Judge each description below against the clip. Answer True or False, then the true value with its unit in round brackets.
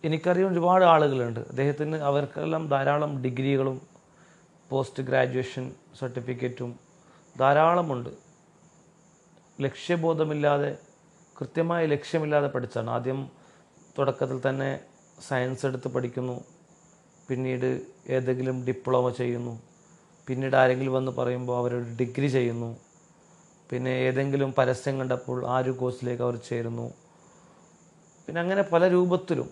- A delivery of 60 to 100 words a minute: True (90 wpm)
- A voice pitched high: False (135 Hz)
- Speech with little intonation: False (4.8 semitones)